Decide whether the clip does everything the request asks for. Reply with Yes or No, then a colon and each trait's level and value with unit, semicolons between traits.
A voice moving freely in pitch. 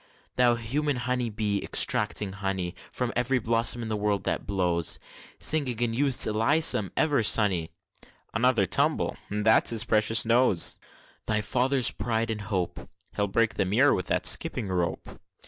No: average, 3.4 semitones